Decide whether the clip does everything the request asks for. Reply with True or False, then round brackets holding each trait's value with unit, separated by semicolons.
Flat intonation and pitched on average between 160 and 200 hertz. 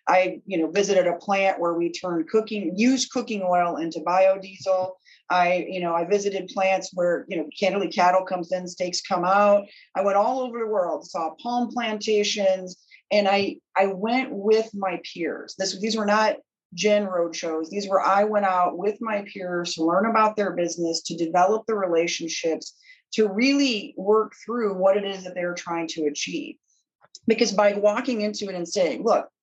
False (3.2 semitones; 190 Hz)